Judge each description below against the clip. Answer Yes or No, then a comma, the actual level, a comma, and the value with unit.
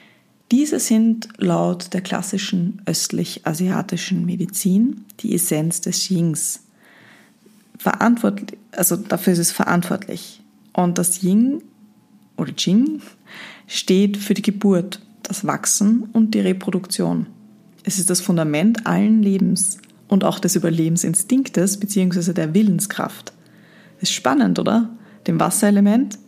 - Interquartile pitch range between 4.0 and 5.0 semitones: No, average, 3.0 semitones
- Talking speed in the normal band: No, slow, 110 wpm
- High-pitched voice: Yes, high, 200 Hz